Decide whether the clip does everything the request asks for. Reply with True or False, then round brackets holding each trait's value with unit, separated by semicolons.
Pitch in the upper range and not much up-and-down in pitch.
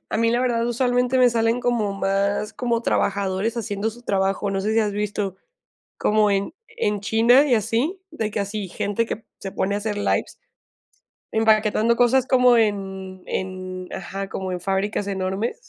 False (210 Hz; 3.0 semitones)